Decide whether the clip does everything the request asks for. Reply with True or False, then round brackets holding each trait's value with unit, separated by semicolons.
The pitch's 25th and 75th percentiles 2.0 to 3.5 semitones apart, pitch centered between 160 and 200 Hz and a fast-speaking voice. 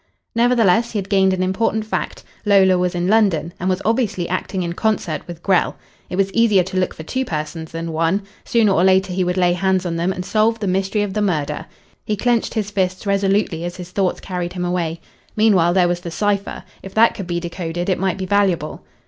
True (2.7 semitones; 185 Hz; 225 wpm)